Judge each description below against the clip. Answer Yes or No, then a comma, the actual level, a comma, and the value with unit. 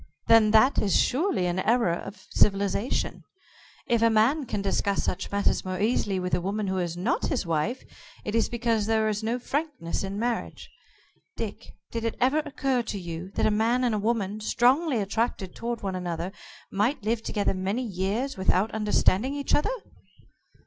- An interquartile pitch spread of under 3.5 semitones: No, average, 3.8 semitones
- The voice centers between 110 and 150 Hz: No, high, 215 Hz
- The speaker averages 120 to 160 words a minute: No, average, 175 wpm